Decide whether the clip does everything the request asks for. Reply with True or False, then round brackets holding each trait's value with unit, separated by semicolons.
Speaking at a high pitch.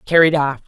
False (150 Hz)